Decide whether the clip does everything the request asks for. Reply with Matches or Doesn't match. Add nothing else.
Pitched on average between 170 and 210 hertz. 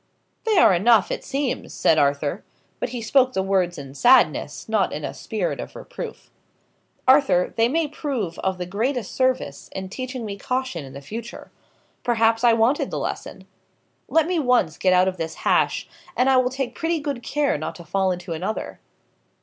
Doesn't match